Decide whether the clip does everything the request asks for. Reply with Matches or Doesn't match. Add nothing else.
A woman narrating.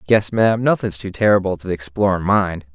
Doesn't match